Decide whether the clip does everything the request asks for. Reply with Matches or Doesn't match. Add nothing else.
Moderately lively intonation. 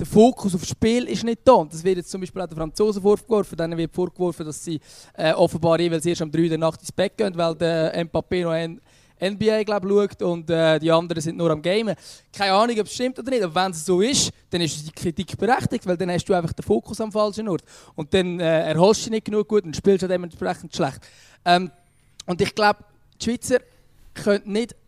Matches